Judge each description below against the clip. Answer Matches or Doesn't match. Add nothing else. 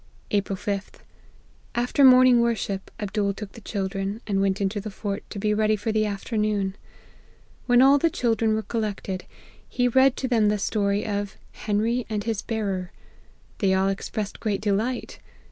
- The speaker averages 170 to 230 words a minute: Matches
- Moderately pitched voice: Doesn't match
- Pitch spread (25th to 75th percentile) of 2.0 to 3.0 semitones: Matches